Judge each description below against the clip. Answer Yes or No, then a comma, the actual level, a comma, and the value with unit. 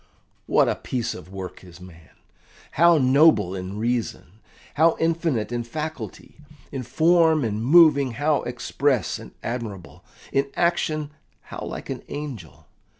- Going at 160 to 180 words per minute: No, average, 140 wpm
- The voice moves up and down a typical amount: No, wide, 6.7 semitones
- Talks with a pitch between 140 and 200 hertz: No, low, 130 Hz